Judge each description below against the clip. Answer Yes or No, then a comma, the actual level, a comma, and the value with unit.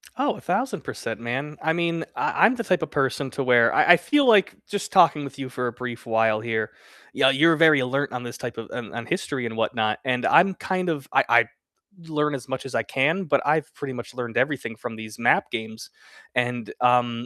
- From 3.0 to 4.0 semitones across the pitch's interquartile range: No, average, 4.7 semitones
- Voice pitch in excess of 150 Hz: No, low, 130 Hz